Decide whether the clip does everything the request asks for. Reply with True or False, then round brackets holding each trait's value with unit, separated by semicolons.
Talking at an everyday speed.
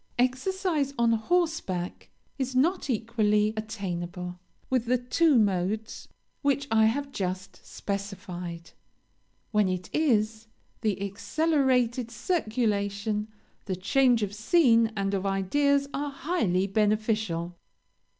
False (105 wpm)